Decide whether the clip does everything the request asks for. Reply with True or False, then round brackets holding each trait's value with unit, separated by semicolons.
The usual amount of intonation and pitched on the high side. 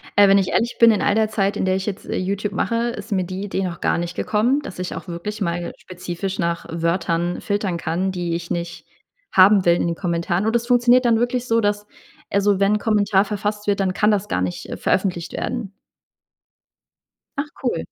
True (3.3 semitones; 195 Hz)